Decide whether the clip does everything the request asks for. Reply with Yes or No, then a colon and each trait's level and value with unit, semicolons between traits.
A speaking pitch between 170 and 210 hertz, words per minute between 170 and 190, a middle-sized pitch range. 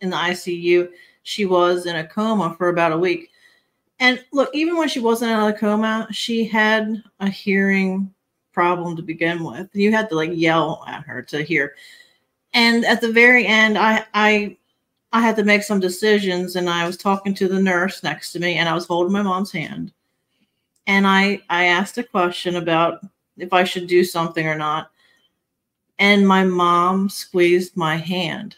Yes: high, 190 Hz; average, 185 wpm; average, 3.6 semitones